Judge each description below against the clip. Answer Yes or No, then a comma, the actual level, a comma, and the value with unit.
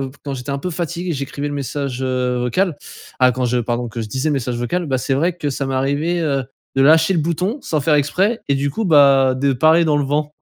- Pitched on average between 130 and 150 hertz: Yes, medium, 140 Hz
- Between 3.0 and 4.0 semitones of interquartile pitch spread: Yes, average, 3.6 semitones